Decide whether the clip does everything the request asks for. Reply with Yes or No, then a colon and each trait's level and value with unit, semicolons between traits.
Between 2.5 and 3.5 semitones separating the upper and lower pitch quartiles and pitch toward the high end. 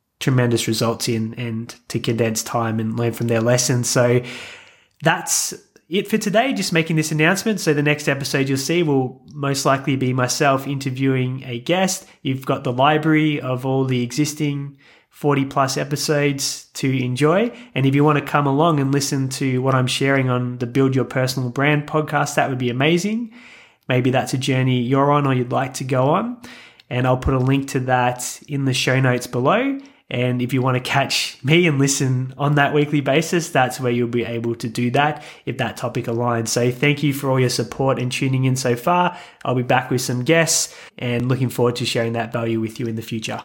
No: average, 3.0 semitones; low, 135 Hz